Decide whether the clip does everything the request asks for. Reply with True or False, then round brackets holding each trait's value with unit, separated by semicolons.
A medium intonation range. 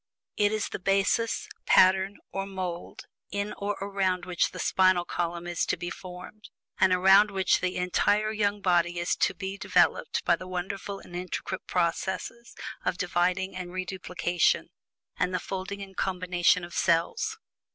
False (1.8 semitones)